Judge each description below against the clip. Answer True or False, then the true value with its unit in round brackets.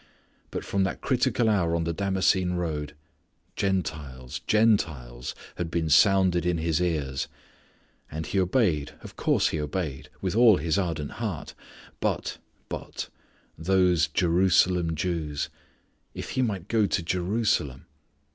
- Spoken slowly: True (130 wpm)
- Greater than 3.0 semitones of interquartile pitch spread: True (3.6 semitones)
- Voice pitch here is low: True (85 Hz)